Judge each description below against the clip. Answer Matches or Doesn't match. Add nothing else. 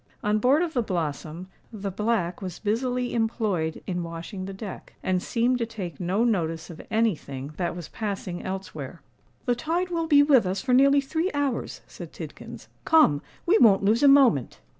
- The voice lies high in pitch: Matches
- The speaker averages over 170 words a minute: Matches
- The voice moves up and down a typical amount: Doesn't match